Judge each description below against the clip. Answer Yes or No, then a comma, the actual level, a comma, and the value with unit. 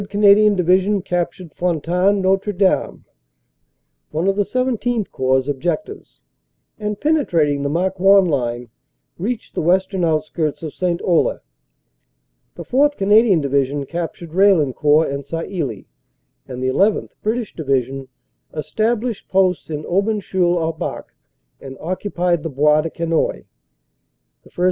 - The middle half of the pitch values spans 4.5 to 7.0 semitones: Yes, average, 5.0 semitones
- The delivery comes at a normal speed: No, slow, 130 wpm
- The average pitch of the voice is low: No, medium, 175 Hz